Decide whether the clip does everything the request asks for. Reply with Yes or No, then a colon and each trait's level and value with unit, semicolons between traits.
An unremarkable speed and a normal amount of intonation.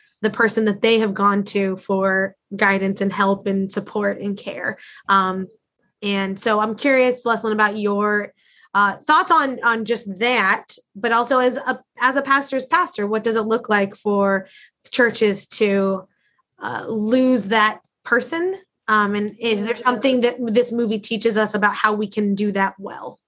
Yes: average, 170 wpm; average, 3.1 semitones